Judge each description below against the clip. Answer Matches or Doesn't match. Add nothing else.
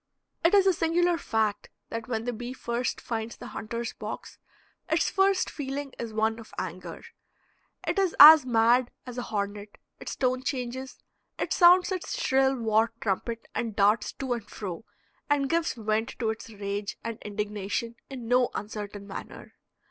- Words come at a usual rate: Matches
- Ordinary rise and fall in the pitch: Matches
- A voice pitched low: Doesn't match